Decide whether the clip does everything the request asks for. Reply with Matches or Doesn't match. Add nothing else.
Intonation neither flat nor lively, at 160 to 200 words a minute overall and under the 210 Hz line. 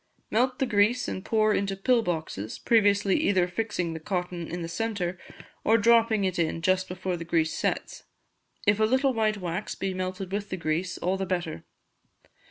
Matches